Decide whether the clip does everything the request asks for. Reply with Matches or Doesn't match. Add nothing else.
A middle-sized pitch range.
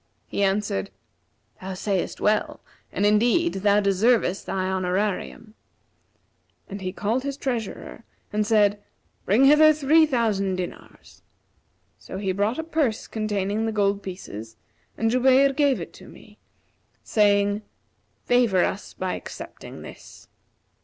Matches